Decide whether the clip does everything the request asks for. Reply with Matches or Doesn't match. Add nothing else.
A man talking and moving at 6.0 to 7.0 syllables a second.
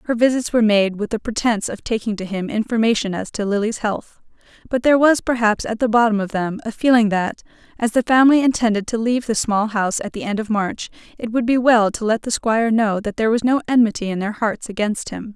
Doesn't match